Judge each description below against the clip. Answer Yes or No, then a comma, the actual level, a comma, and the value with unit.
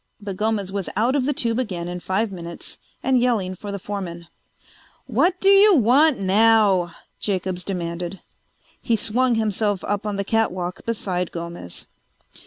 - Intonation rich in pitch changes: No, average, 4.1 semitones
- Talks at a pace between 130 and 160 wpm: Yes, average, 155 wpm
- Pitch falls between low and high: No, high, 205 Hz